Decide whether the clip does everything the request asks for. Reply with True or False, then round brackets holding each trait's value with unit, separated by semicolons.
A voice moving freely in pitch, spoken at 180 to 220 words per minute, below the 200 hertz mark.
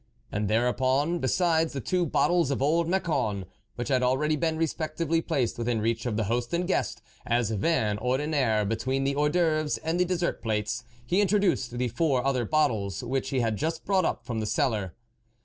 True (5.8 semitones; 195 wpm; 135 Hz)